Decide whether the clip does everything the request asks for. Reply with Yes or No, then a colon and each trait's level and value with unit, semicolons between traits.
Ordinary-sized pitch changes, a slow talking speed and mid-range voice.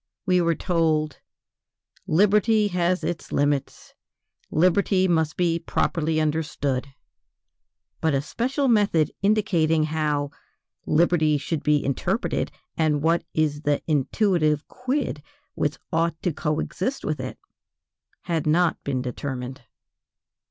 Yes: average, 3.3 semitones; slow, 115 wpm; medium, 160 Hz